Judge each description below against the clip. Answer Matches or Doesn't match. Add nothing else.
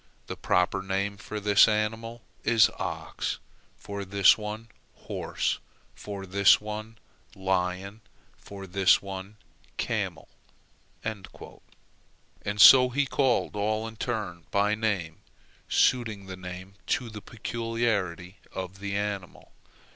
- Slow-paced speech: Matches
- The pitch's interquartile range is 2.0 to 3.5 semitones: Matches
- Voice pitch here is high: Doesn't match